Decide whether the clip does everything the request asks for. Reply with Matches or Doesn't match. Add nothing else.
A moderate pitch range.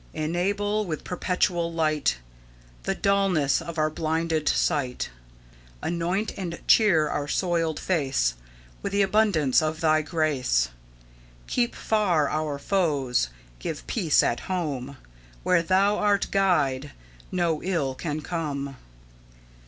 Matches